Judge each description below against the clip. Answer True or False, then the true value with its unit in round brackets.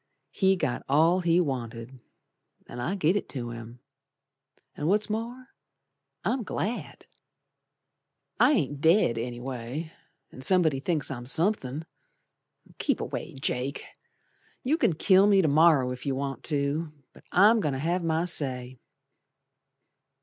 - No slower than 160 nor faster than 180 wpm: False (135 wpm)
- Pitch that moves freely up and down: True (6.1 semitones)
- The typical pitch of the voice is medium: True (150 Hz)